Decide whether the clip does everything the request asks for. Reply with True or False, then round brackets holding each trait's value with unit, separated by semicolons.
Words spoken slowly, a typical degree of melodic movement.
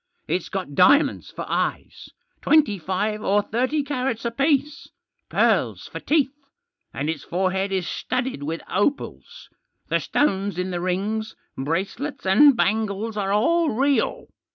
False (130 wpm; 6.3 semitones)